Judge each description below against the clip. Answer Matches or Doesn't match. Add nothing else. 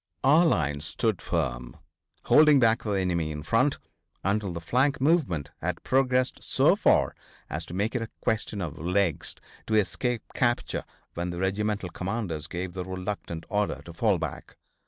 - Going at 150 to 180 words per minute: Matches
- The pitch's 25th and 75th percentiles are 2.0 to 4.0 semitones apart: Doesn't match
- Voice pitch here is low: Matches